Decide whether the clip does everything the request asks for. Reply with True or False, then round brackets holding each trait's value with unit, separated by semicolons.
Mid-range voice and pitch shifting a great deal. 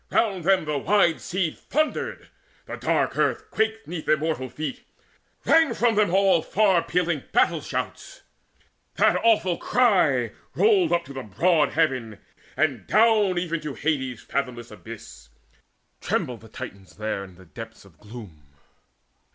True (160 Hz; 8.2 semitones)